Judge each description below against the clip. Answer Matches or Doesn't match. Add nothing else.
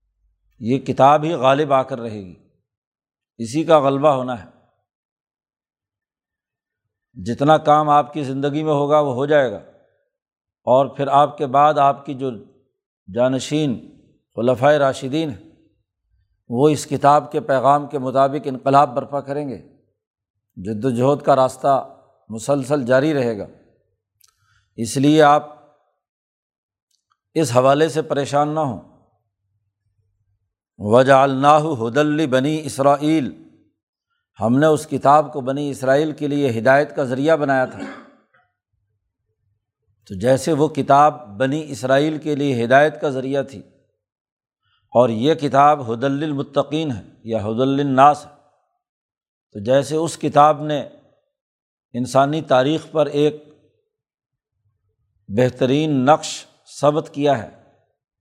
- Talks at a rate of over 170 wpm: Doesn't match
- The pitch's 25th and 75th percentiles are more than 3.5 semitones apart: Matches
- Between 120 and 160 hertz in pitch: Matches